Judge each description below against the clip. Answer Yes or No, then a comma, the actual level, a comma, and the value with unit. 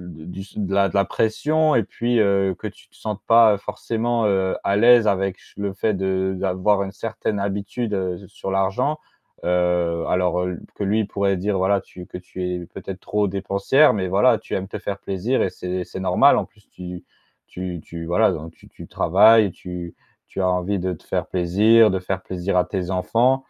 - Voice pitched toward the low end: Yes, very low, 95 Hz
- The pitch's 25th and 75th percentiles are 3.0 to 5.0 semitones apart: No, narrow, 2.6 semitones